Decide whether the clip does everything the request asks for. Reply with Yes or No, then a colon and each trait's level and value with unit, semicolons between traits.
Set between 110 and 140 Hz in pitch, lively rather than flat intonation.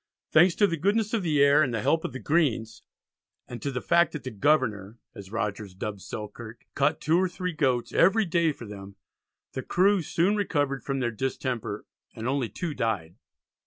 Yes: low, 135 Hz; wide, 7.1 semitones